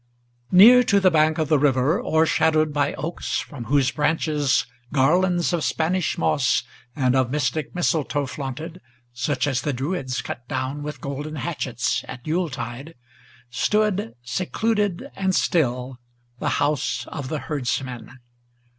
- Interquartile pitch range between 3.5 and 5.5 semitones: Yes, average, 4.2 semitones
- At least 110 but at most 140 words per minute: Yes, slow, 135 wpm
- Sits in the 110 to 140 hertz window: No, medium, 150 Hz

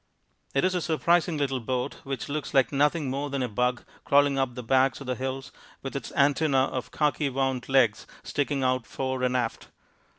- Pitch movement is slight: Yes, narrow, 2.0 semitones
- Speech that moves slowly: No, average, 195 wpm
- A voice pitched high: No, low, 135 Hz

